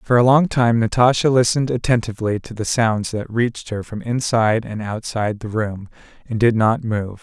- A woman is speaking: No, male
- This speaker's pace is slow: No, average, 190 wpm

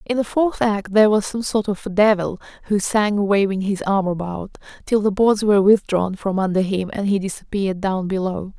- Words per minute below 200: No, fast, 205 wpm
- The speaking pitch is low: No, high, 200 Hz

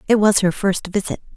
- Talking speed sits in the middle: No, fast, 220 wpm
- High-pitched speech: Yes, high, 200 Hz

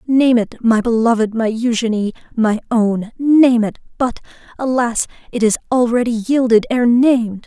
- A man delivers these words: No, female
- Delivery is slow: Yes, slow, 130 wpm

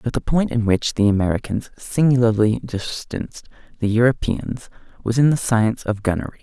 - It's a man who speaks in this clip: Yes, male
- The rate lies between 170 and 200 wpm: No, average, 160 wpm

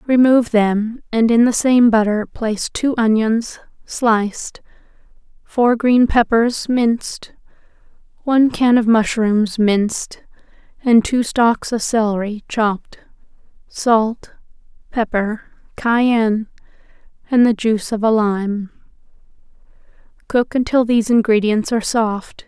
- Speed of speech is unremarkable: No, slow, 110 wpm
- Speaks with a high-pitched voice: Yes, high, 225 Hz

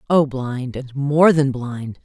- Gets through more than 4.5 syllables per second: No, 3.3 syllables/s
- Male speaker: No, female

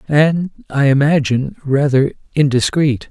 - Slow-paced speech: Yes, slow, 60 wpm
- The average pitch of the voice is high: No, medium, 140 Hz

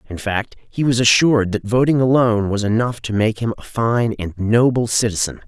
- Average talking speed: Yes, average, 195 wpm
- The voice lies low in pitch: Yes, low, 115 Hz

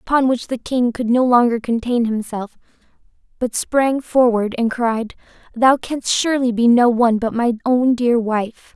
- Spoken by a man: No, female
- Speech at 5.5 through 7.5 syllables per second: No, 4.4 syllables/s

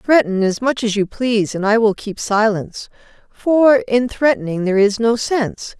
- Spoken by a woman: Yes, female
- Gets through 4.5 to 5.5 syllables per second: Yes, 4.9 syllables/s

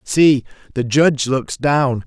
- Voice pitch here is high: No, low, 135 Hz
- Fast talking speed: No, average, 145 wpm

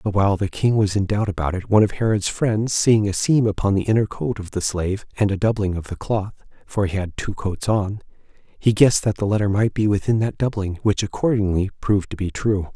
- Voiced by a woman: No, male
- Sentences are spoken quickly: Yes, fast, 240 wpm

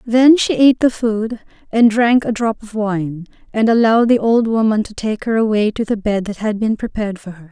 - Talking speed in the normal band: No, fast, 230 wpm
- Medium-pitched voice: No, high, 220 Hz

